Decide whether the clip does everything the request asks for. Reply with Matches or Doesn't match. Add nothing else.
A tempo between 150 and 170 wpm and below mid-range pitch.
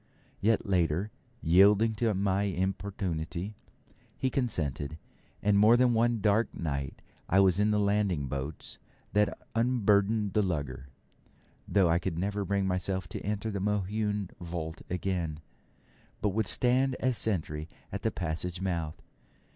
Doesn't match